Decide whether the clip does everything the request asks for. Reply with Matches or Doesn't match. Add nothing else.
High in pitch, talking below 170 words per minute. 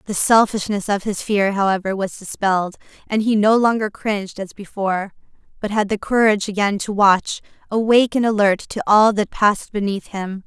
Doesn't match